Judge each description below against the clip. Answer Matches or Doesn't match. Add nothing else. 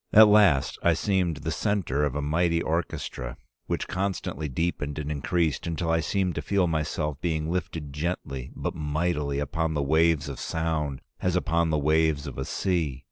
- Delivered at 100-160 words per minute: Doesn't match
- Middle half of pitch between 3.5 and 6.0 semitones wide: Doesn't match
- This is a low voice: Matches